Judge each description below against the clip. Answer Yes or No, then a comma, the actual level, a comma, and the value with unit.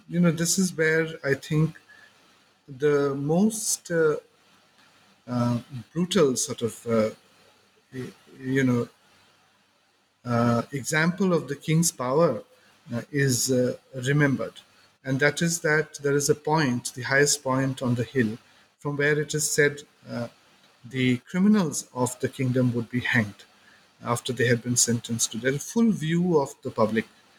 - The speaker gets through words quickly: No, average, 145 wpm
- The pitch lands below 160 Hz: Yes, low, 135 Hz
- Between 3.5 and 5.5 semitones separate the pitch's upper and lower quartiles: Yes, average, 4.2 semitones